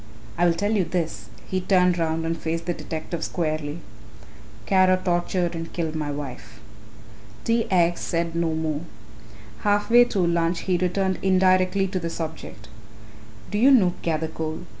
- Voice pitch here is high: No, medium, 170 Hz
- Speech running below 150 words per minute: No, average, 155 wpm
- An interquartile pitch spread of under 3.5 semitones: Yes, narrow, 2.6 semitones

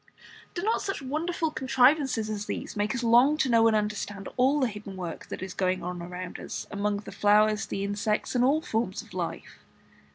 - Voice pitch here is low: No, high, 215 Hz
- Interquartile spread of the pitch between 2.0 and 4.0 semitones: No, average, 4.6 semitones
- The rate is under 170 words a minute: No, average, 200 wpm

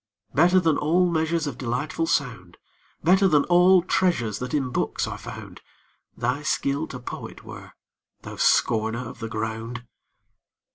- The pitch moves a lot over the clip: Yes, wide, 6.1 semitones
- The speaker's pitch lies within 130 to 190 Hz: Yes, medium, 140 Hz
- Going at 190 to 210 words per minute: No, average, 145 wpm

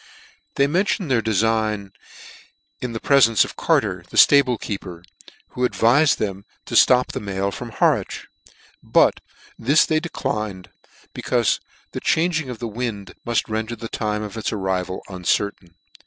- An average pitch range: Yes, average, 4.1 semitones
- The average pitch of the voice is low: Yes, low, 110 Hz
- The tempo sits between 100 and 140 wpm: No, average, 150 wpm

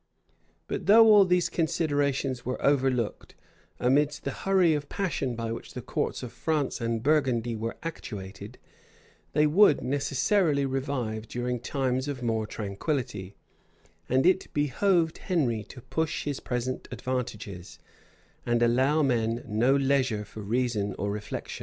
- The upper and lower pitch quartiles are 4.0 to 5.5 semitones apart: Yes, average, 4.3 semitones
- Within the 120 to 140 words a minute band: Yes, slow, 135 wpm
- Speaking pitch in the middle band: No, low, 130 Hz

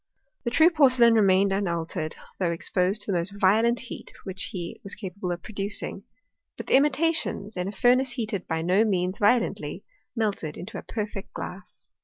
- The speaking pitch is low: No, high, 200 Hz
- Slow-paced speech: No, average, 175 wpm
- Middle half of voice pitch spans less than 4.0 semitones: No, average, 4.3 semitones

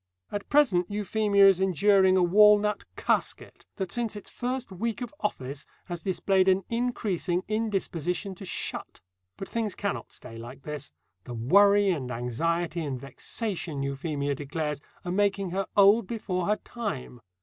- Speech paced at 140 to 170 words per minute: Yes, average, 150 wpm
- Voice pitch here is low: No, high, 190 Hz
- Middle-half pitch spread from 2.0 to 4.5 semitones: No, average, 5.2 semitones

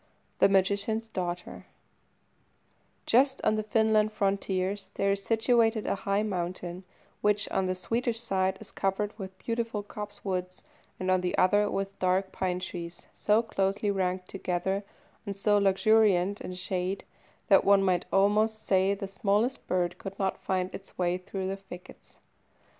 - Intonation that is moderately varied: No, narrow, 2.1 semitones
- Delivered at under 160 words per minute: Yes, average, 150 wpm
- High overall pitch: Yes, high, 195 Hz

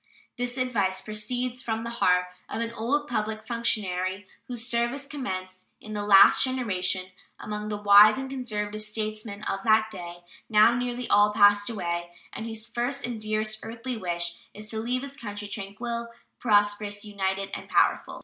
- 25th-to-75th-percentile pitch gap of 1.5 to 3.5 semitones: Yes, narrow, 2.6 semitones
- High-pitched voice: Yes, high, 215 Hz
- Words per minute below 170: Yes, average, 160 wpm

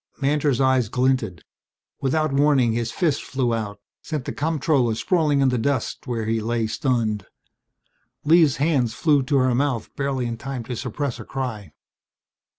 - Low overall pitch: Yes, low, 130 Hz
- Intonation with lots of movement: No, average, 3.6 semitones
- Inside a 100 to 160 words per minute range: Yes, average, 155 wpm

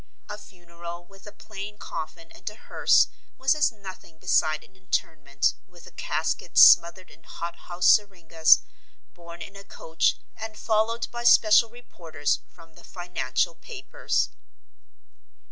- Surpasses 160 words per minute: No, average, 140 wpm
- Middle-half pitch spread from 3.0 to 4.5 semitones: Yes, average, 4.1 semitones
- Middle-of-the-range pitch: Yes, medium, 175 Hz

